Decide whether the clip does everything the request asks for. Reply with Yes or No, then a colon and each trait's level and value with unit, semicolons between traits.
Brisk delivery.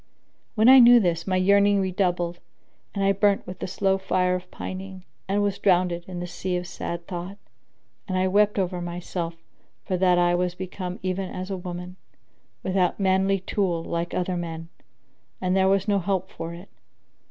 No: average, 180 wpm